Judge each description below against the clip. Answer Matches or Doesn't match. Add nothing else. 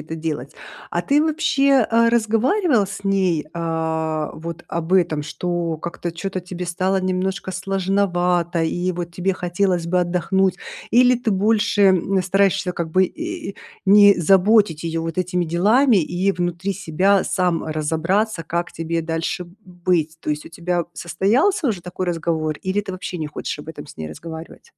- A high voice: Doesn't match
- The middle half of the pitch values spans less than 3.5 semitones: Matches